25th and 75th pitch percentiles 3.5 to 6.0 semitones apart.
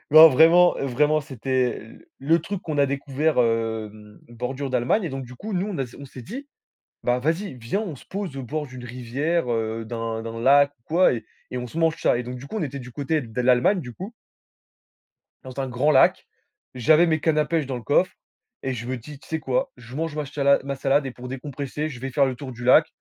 Yes: average, 4.0 semitones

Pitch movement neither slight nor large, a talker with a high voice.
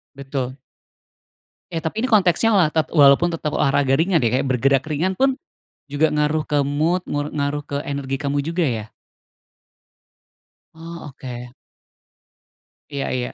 No: average, 3.2 semitones; medium, 145 Hz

